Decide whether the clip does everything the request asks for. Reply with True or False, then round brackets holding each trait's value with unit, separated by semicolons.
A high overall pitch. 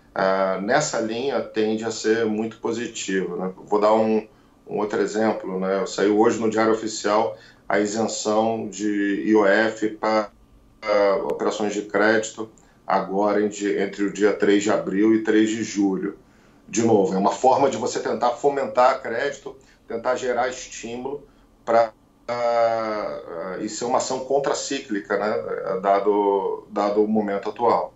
False (110 Hz)